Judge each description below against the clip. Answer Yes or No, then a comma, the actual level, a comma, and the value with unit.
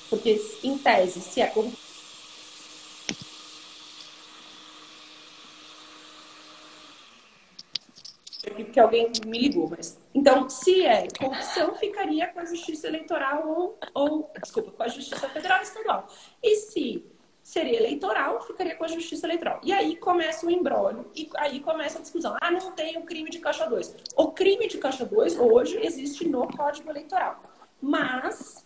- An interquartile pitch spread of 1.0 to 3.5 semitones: No, average, 4.9 semitones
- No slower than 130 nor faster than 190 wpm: Yes, average, 140 wpm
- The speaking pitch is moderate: No, very high, 320 Hz